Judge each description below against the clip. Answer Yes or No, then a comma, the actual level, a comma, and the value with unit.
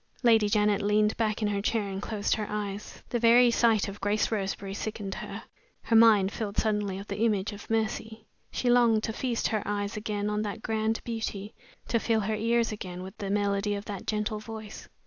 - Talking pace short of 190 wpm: No, fast, 205 wpm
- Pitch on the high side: Yes, high, 210 Hz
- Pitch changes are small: Yes, narrow, 1.6 semitones